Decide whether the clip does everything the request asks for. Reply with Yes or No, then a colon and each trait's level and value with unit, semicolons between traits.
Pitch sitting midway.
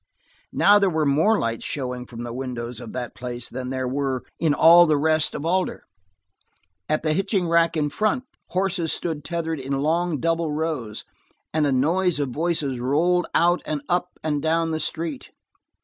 Yes: medium, 155 Hz